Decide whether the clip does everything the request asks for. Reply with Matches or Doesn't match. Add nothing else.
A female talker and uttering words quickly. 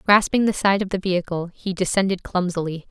Doesn't match